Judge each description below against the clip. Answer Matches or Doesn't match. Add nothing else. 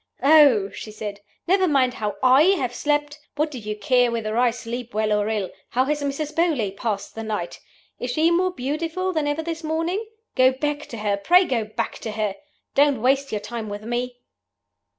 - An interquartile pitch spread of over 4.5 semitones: Matches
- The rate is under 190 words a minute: Doesn't match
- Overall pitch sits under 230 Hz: Doesn't match